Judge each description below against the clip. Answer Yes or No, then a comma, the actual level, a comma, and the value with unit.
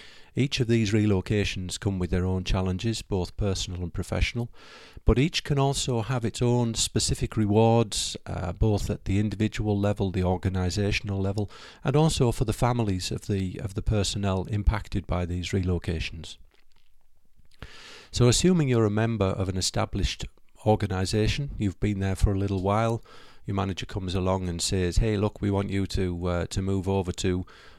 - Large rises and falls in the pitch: No, average, 3.2 semitones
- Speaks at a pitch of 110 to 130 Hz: No, low, 100 Hz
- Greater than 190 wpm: No, average, 170 wpm